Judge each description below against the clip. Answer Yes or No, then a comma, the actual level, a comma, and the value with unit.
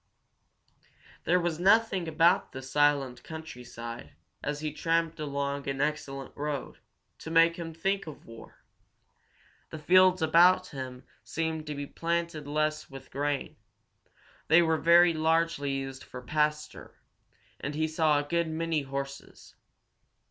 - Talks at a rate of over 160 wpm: No, slow, 135 wpm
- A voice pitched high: No, medium, 155 Hz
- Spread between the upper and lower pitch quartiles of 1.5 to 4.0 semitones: Yes, average, 2.9 semitones